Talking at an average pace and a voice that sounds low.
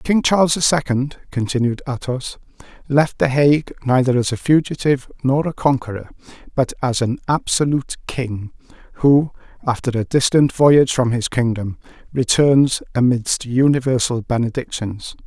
No: slow, 130 wpm; low, 130 Hz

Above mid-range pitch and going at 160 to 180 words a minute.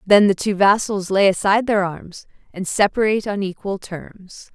Yes: high, 195 Hz; average, 170 wpm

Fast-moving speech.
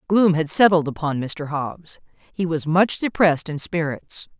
No: average, 165 wpm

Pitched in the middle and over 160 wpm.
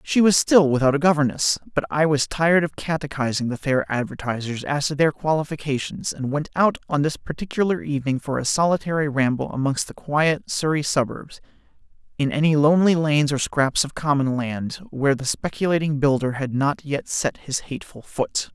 Yes: medium, 145 Hz; average, 180 wpm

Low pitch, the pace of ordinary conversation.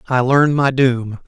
Yes: low, 130 Hz; average, 190 wpm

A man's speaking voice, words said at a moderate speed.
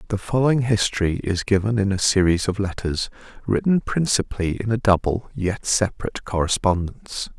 Yes: male; average, 145 wpm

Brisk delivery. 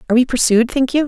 Yes: fast, 280 wpm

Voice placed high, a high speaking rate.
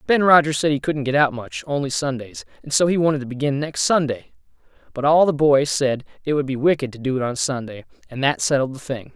No: medium, 140 Hz; fast, 240 wpm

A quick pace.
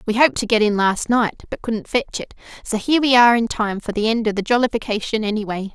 Yes: fast, 250 wpm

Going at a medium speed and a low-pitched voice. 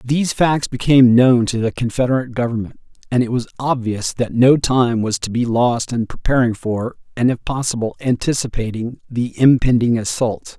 Yes: average, 165 wpm; low, 120 Hz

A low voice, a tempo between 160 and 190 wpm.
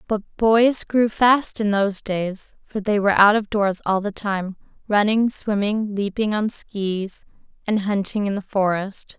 No: high, 205 Hz; average, 170 wpm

